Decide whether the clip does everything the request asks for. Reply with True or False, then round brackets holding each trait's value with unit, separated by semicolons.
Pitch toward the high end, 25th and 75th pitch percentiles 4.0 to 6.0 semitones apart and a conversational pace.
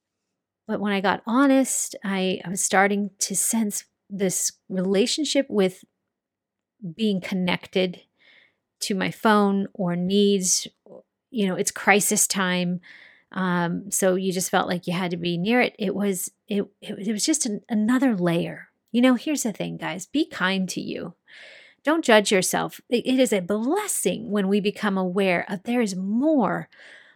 False (200 Hz; 3.5 semitones; 170 wpm)